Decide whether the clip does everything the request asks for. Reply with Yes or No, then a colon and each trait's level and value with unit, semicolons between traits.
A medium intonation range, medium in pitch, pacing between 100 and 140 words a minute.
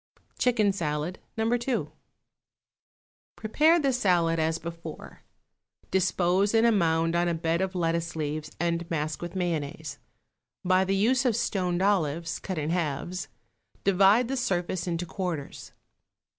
Yes: average, 3.4 semitones; medium, 175 Hz; slow, 135 wpm